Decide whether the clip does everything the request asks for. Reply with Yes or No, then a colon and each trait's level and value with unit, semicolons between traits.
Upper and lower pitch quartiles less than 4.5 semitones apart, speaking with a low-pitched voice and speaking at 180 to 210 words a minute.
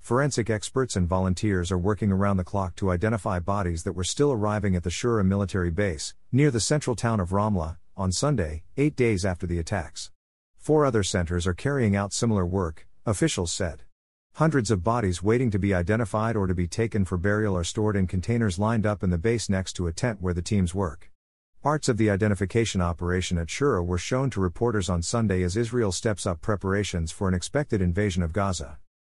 Yes: average, 4.0 semitones; low, 100 Hz; fast, 205 wpm